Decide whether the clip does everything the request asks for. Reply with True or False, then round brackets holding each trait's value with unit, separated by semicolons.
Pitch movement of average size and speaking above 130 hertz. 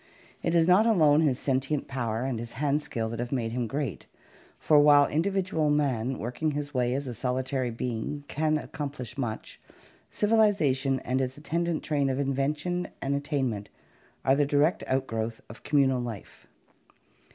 True (3.2 semitones; 140 Hz)